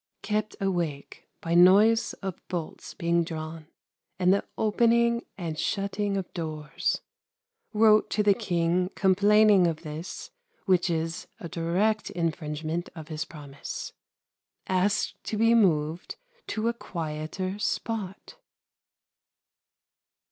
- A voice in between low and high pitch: Yes, medium, 180 Hz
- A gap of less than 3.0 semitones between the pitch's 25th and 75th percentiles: No, average, 4.3 semitones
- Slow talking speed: Yes, slow, 110 wpm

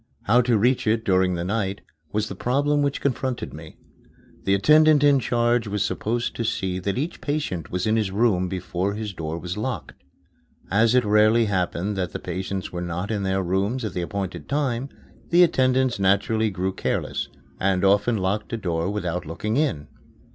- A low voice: Yes, low, 105 Hz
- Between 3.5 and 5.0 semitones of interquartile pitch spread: Yes, average, 4.4 semitones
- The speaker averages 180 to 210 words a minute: Yes, average, 185 wpm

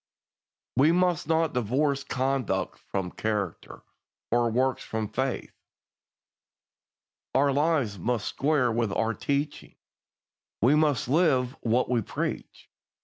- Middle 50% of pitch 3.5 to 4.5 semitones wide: Yes, average, 4.1 semitones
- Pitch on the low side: Yes, low, 130 Hz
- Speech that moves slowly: Yes, slow, 110 wpm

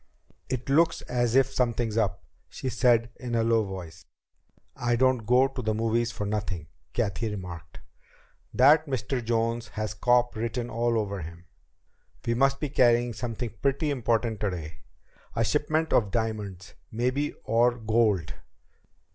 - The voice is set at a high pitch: No, low, 115 Hz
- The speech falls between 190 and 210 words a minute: No, average, 145 wpm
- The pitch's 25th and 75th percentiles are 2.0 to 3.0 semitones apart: Yes, average, 2.7 semitones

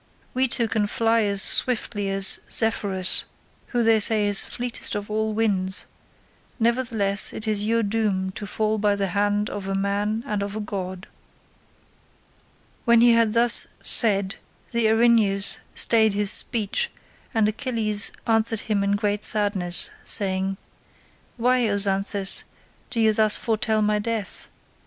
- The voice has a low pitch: No, high, 210 Hz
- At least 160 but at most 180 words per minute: No, average, 145 wpm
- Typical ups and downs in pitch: No, narrow, 2.1 semitones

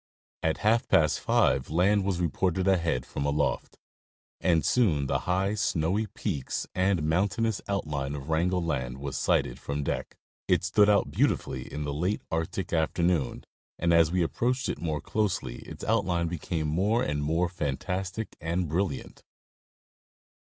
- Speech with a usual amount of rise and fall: Yes, average, 4.4 semitones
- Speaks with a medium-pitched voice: No, very low, 85 Hz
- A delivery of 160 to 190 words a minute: No, average, 150 wpm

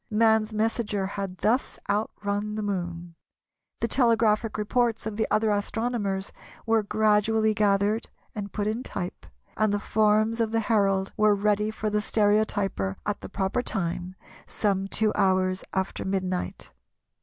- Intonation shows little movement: Yes, narrow, 1.9 semitones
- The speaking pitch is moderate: No, high, 210 Hz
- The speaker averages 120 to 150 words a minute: Yes, average, 145 wpm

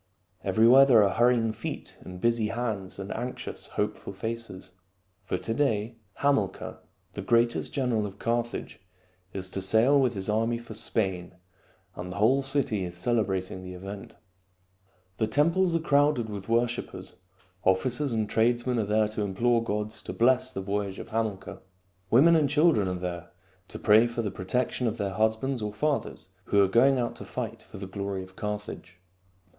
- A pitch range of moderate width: Yes, average, 3.7 semitones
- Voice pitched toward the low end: Yes, low, 110 Hz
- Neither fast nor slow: Yes, average, 170 wpm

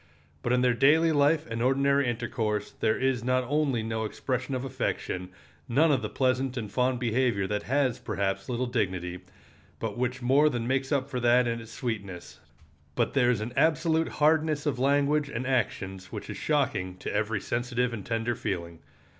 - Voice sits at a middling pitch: No, low, 125 Hz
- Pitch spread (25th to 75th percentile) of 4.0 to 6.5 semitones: No, average, 3.5 semitones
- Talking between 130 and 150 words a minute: No, average, 180 wpm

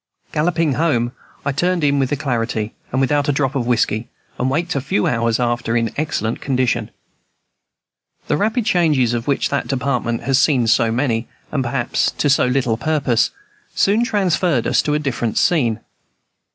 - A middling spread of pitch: Yes, average, 4.2 semitones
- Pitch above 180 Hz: No, low, 135 Hz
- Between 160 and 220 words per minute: Yes, average, 165 wpm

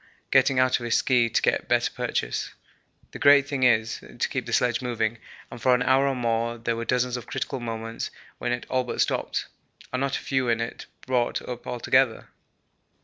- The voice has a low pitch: Yes, low, 125 Hz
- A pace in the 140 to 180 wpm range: No, fast, 205 wpm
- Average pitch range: No, narrow, 1.7 semitones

